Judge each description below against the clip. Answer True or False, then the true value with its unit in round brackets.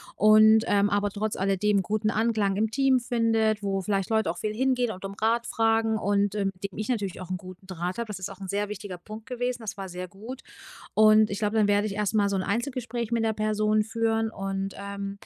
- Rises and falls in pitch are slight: True (2.1 semitones)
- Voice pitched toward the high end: True (210 Hz)